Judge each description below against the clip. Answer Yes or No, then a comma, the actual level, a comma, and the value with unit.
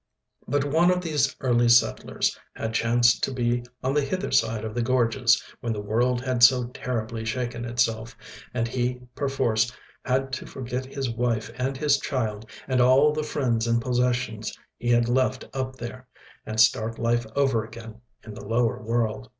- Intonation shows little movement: Yes, narrow, 2.2 semitones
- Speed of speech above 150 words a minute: Yes, average, 175 wpm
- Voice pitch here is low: Yes, low, 120 Hz